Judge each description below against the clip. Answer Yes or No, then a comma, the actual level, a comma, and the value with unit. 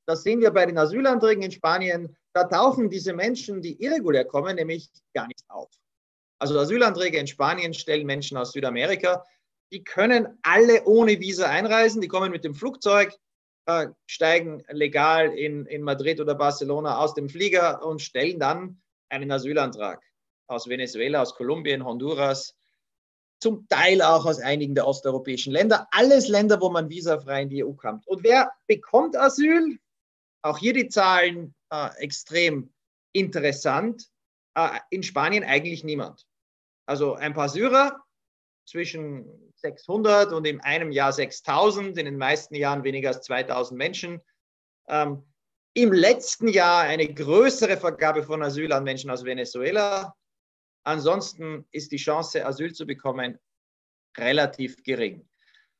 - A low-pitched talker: No, medium, 160 Hz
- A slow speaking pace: No, average, 145 wpm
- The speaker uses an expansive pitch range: Yes, wide, 5.7 semitones